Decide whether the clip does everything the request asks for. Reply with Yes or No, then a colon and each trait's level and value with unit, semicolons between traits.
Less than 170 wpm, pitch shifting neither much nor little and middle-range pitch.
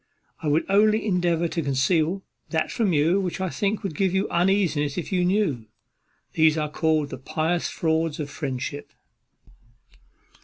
Yes: average, 155 wpm; average, 3.9 semitones; medium, 165 Hz